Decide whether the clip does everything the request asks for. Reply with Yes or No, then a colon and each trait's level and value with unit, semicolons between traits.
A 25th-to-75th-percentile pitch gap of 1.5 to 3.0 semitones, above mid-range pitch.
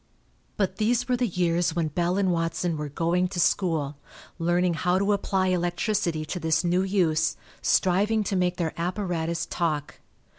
No: narrow, 2.4 semitones; medium, 175 Hz